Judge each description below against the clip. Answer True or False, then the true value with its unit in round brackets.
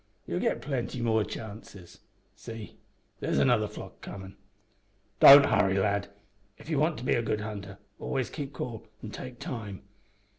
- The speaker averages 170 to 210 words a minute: False (155 wpm)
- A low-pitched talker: True (110 Hz)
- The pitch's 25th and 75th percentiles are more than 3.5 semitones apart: True (4.0 semitones)